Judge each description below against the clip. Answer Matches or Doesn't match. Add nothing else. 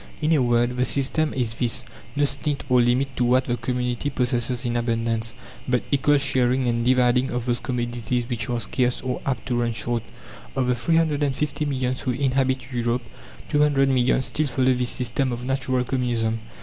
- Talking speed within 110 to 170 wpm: Doesn't match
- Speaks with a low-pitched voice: Matches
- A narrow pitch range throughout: Matches